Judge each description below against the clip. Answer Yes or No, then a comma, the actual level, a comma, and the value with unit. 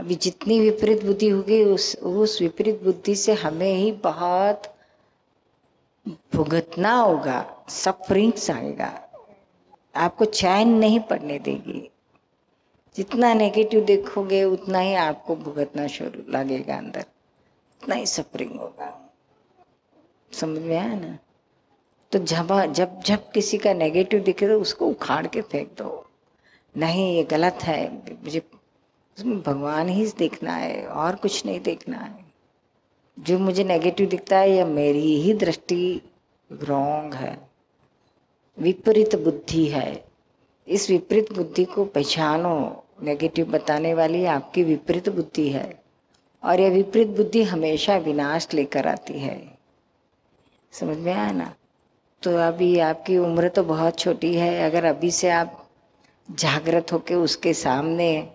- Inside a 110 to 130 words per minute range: Yes, average, 125 wpm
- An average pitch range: Yes, average, 4.2 semitones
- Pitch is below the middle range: No, medium, 175 Hz